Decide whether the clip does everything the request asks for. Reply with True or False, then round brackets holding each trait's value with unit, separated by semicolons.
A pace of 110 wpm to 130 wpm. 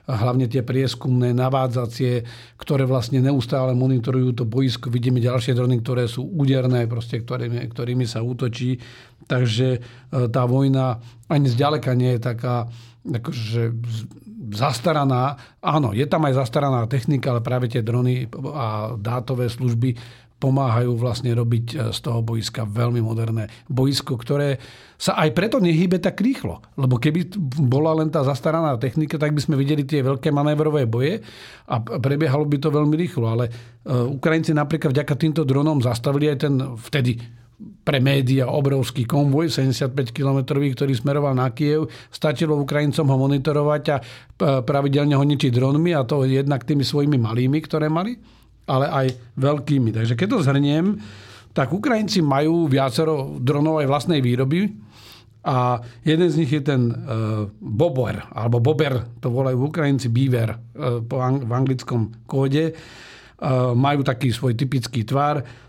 False (140 wpm)